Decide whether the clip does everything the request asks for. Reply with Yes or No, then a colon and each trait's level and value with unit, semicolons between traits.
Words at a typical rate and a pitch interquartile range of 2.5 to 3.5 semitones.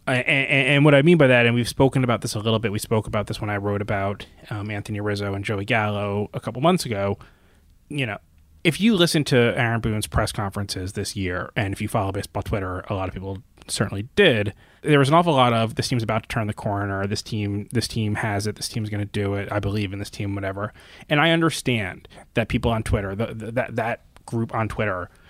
No: fast, 240 wpm; average, 3.2 semitones